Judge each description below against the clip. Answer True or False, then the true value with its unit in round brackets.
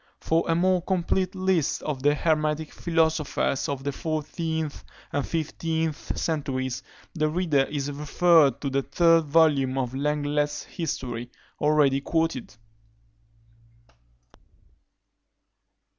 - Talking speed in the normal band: False (105 wpm)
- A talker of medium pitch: True (150 Hz)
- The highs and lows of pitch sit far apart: False (2.8 semitones)